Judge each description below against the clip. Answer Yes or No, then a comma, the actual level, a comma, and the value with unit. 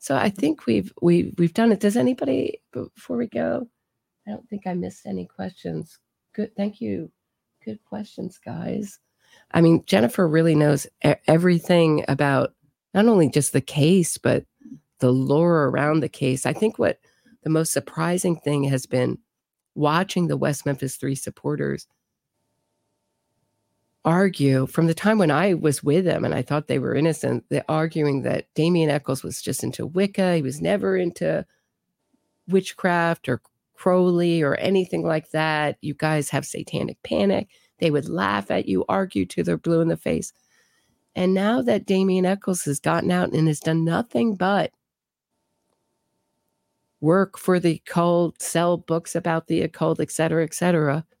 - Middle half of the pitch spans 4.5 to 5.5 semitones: No, average, 4.1 semitones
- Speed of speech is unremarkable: Yes, average, 160 wpm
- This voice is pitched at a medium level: Yes, medium, 165 Hz